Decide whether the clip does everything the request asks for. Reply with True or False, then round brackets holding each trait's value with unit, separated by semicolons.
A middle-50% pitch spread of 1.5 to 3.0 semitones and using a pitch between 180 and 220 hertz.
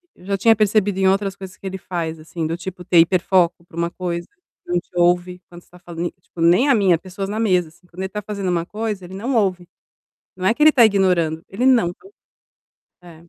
True (2.5 semitones; 185 Hz)